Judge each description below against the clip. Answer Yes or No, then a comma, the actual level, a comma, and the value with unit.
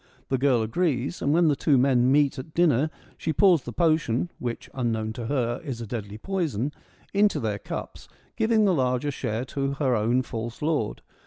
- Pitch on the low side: Yes, low, 130 Hz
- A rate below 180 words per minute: No, average, 185 wpm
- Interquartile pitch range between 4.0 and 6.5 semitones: Yes, average, 4.9 semitones